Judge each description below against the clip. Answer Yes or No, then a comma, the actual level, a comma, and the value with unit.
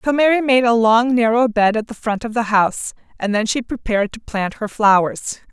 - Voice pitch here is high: Yes, high, 225 Hz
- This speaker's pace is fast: Yes, fast, 230 wpm